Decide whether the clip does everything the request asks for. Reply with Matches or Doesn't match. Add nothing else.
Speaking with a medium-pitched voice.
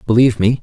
Doesn't match